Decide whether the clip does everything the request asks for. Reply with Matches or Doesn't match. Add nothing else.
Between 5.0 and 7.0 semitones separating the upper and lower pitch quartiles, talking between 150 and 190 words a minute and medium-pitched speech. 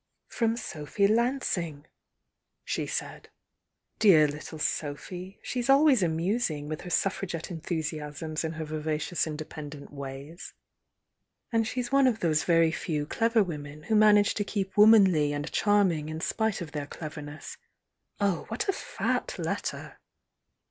Doesn't match